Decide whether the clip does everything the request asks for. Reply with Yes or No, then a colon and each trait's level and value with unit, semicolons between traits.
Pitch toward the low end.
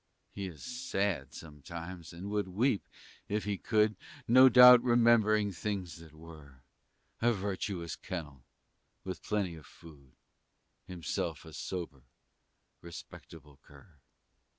Yes: very low, 90 Hz